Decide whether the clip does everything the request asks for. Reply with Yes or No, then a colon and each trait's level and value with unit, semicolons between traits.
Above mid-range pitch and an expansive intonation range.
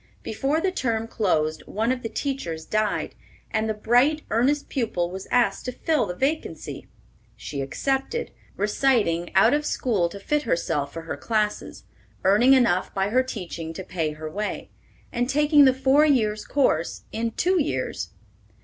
Yes: high, 225 Hz; wide, 7.1 semitones